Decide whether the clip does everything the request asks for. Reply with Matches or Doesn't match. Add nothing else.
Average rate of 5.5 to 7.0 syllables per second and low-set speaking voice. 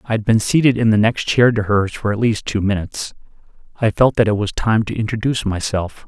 Matches